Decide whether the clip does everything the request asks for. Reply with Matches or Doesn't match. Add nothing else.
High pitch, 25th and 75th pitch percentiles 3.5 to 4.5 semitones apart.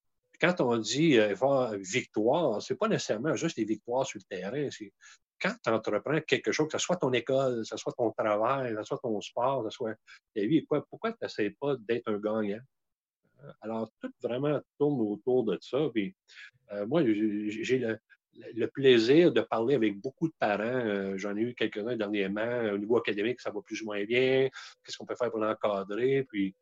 Doesn't match